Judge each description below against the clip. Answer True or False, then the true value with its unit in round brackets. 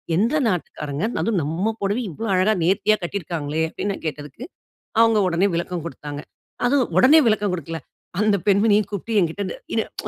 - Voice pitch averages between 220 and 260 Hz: False (195 Hz)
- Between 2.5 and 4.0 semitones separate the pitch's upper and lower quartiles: False (4.6 semitones)